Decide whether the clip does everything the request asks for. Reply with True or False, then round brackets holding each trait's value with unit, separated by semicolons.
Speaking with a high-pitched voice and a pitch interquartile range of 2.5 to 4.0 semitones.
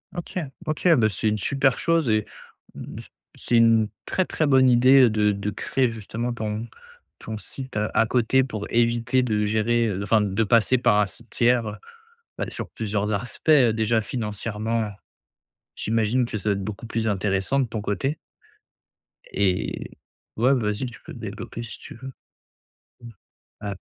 False (115 Hz; 2.9 semitones)